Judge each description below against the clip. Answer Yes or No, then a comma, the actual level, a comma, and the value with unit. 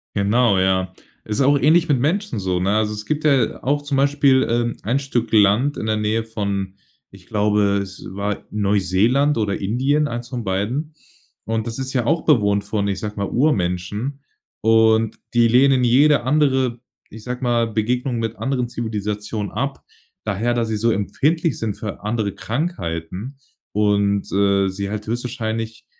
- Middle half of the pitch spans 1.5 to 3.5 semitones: No, average, 4.4 semitones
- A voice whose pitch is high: No, low, 115 Hz